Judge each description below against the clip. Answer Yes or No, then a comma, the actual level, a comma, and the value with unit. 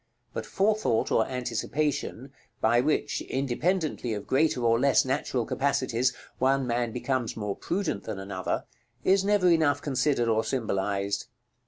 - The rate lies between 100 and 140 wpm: Yes, slow, 135 wpm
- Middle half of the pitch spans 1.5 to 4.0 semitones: No, average, 4.5 semitones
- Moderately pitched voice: No, low, 130 Hz